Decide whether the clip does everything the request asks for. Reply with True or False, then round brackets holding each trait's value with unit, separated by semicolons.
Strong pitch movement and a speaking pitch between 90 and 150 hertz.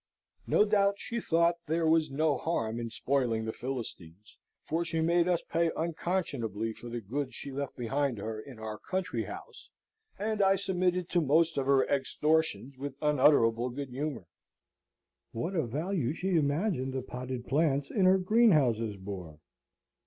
True (5.9 semitones; 140 Hz)